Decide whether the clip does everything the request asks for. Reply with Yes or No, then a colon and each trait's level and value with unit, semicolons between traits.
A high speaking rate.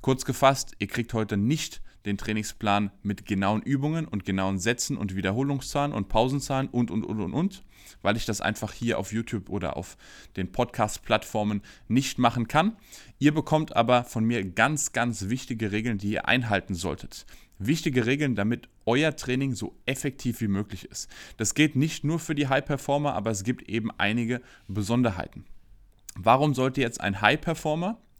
No: average, 165 wpm